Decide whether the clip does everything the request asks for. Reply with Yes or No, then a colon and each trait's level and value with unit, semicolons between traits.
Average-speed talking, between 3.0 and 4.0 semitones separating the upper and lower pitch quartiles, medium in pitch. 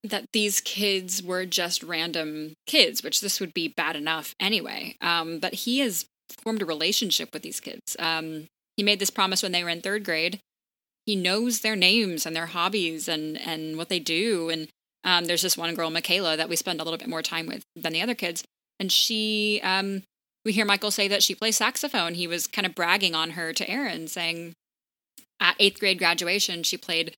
No: fast, 210 wpm; average, 3.7 semitones; medium, 180 Hz